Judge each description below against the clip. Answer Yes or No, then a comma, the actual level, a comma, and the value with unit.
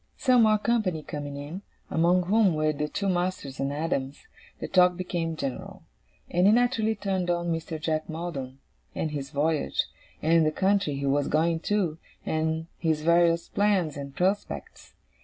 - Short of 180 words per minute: Yes, average, 160 wpm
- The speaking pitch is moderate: Yes, medium, 165 Hz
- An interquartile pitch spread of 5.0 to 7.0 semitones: No, average, 3.5 semitones